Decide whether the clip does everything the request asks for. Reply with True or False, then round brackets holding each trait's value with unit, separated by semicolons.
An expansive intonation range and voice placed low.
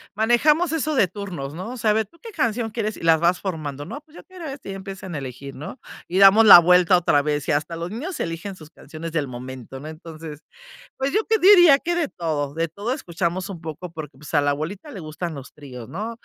False (6.6 semitones; 180 Hz)